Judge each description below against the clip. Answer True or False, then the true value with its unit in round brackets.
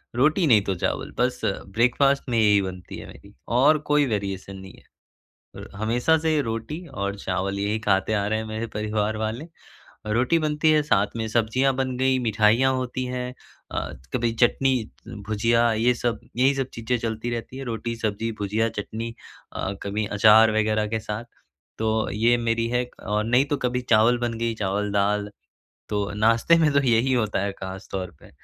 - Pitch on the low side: True (115 Hz)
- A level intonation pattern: False (3.1 semitones)